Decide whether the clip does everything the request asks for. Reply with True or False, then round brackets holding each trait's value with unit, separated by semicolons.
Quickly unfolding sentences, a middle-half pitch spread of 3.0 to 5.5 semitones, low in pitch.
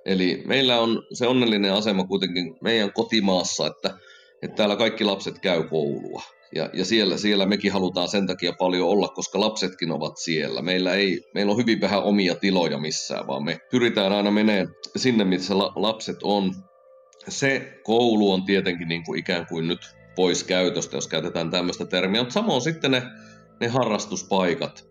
True (170 wpm; 3.5 semitones; 100 Hz)